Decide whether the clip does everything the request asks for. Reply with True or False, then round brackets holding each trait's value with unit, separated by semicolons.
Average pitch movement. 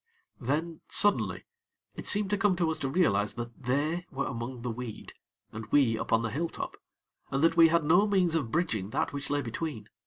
False (6.2 semitones)